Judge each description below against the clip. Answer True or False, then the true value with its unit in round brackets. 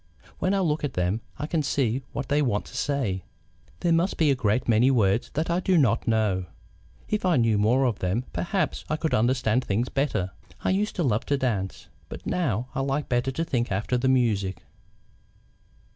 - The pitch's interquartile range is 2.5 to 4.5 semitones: False (5.4 semitones)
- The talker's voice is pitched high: False (125 Hz)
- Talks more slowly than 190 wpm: False (200 wpm)